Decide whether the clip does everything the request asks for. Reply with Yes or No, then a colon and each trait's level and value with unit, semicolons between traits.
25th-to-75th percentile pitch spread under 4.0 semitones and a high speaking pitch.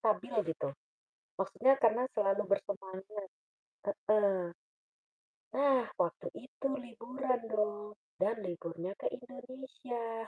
No: average, 4.4 semitones; high, 215 Hz